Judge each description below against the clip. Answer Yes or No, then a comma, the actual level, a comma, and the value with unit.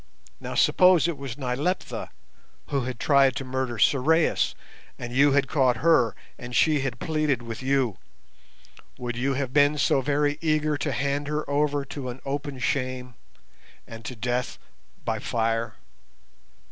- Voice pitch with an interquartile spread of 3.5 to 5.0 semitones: No, average, 2.8 semitones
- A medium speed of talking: Yes, average, 150 wpm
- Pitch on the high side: No, low, 135 Hz